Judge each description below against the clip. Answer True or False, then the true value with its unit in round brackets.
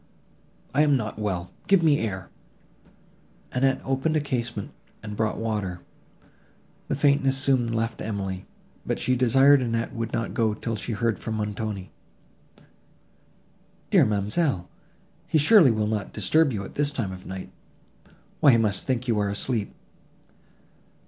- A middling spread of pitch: True (4.3 semitones)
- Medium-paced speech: True (145 wpm)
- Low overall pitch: True (115 Hz)